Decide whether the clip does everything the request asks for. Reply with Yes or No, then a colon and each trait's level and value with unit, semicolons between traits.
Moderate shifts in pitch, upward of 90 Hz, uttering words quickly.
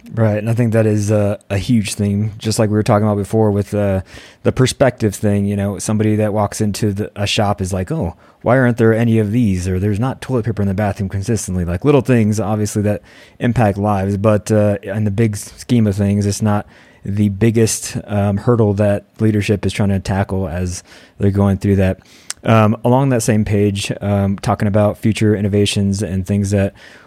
No: narrow, 1.8 semitones; low, 105 Hz; fast, 210 wpm